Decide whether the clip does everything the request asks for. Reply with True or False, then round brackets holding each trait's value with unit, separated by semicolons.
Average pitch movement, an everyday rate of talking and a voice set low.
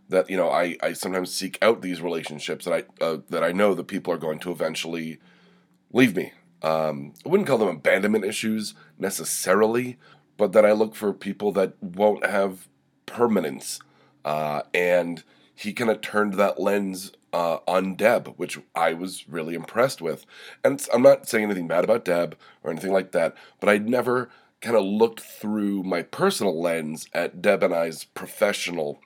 True (4.0 semitones; 180 wpm; 95 Hz)